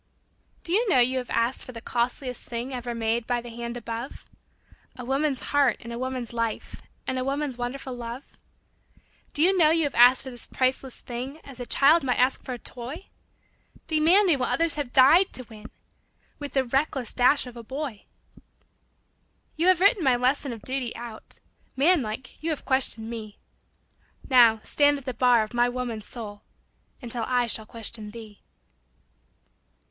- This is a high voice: Yes, very high, 250 Hz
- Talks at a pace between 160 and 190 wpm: Yes, average, 180 wpm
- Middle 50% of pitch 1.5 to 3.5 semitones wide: Yes, average, 2.9 semitones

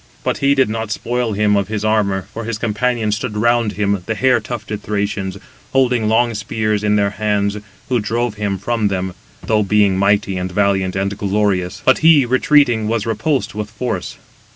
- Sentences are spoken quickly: No, average, 180 wpm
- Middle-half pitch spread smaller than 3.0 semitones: Yes, narrow, 2.5 semitones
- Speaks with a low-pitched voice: Yes, low, 105 Hz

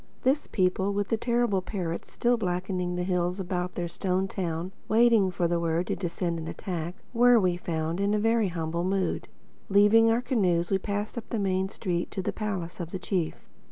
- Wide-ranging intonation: No, average, 3.1 semitones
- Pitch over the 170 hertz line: Yes, medium, 185 Hz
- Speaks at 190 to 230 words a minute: Yes, average, 195 wpm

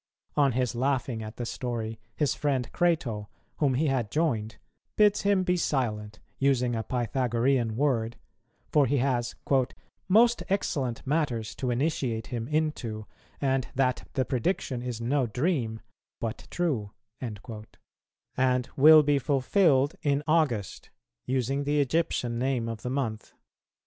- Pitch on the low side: Yes, low, 130 Hz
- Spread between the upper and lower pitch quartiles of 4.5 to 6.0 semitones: No, average, 3.8 semitones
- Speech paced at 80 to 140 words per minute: Yes, slow, 135 wpm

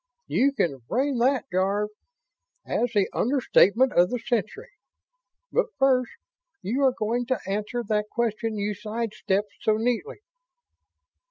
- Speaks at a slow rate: Yes, slow, 125 wpm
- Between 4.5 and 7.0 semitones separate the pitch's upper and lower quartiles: No, average, 3.3 semitones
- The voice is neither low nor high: No, high, 225 Hz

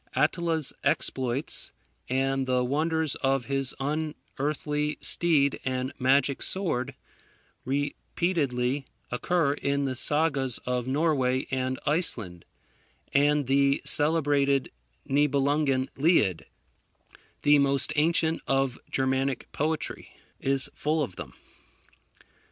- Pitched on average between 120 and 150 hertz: Yes, medium, 140 Hz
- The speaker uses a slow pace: Yes, slow, 95 wpm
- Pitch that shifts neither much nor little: No, narrow, 2.2 semitones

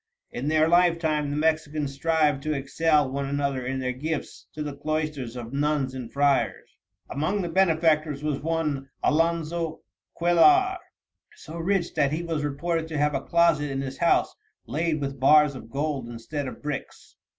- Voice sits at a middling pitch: Yes, medium, 150 Hz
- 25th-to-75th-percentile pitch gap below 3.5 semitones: Yes, average, 2.8 semitones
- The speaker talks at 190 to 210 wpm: No, average, 165 wpm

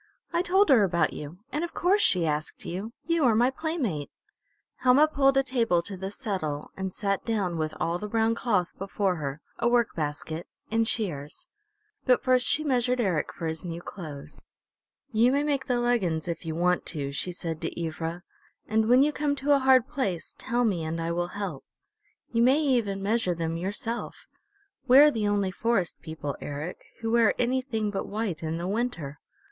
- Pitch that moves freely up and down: Yes, wide, 6.8 semitones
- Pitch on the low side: No, high, 205 Hz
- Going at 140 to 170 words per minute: No, average, 190 wpm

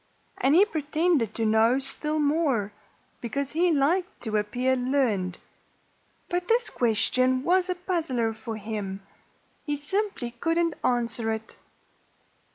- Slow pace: Yes, slow, 125 wpm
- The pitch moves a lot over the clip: Yes, wide, 6.7 semitones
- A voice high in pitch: Yes, very high, 260 Hz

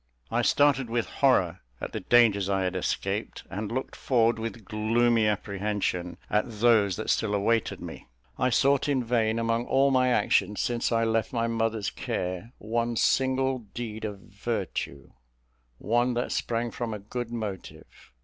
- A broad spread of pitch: No, narrow, 2.6 semitones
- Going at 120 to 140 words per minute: No, average, 160 wpm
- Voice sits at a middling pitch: No, low, 115 Hz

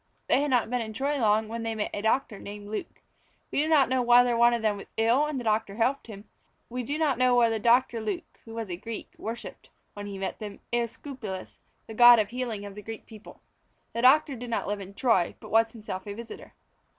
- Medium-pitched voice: No, high, 230 Hz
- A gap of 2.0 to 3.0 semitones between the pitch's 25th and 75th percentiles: Yes, average, 2.7 semitones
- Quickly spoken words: Yes, fast, 235 wpm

